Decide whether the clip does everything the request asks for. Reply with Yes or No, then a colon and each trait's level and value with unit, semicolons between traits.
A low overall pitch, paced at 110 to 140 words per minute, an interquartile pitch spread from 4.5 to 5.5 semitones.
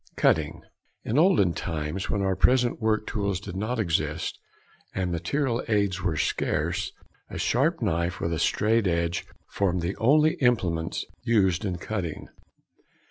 Yes: low, 100 Hz; slow, 135 wpm; average, 5.0 semitones